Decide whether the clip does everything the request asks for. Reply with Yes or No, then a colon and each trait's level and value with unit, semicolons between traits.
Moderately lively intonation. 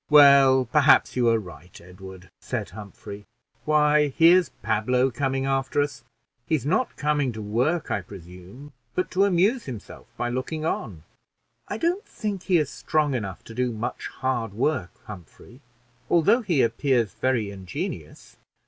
No: wide, 5.9 semitones